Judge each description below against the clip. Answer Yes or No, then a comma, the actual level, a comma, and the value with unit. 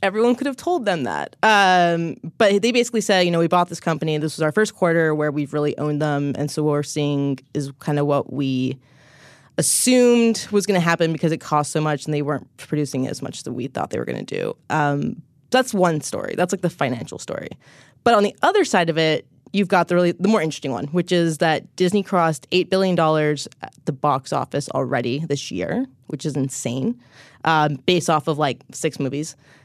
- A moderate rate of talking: No, fast, 225 wpm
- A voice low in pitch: No, medium, 155 Hz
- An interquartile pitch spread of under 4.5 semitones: Yes, average, 3.9 semitones